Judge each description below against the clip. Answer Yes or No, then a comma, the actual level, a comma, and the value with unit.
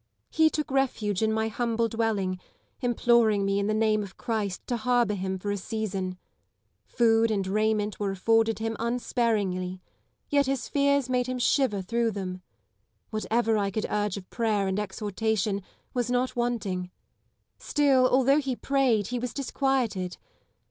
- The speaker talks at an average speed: Yes, average, 155 wpm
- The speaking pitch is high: Yes, high, 220 Hz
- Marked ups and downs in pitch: No, average, 3.4 semitones